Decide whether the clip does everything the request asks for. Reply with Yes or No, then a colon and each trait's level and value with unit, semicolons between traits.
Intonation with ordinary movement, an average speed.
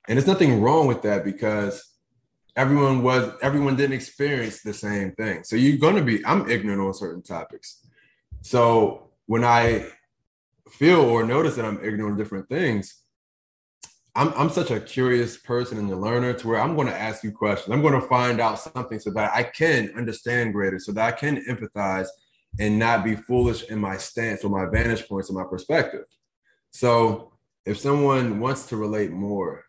Yes: average, 3.4 semitones; average, 185 wpm